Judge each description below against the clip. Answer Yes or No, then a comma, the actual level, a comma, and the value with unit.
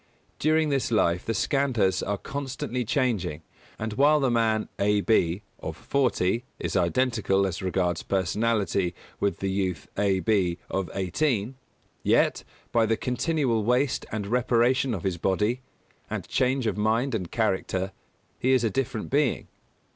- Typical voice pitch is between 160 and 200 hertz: No, low, 110 Hz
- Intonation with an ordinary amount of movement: Yes, average, 4.8 semitones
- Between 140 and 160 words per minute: Yes, average, 145 wpm